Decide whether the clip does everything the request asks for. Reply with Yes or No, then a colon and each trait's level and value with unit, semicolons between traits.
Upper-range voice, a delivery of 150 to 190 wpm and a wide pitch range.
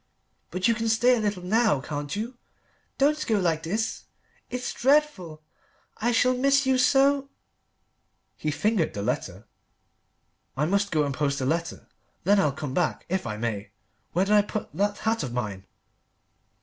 Yes: high, 200 Hz; average, 170 wpm; wide, 7.7 semitones